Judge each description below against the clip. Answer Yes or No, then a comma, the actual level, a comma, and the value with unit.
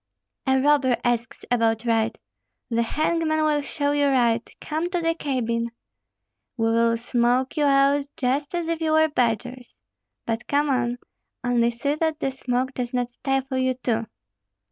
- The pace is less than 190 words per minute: Yes, average, 160 wpm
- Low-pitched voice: No, very high, 260 Hz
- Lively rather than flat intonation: No, average, 3.5 semitones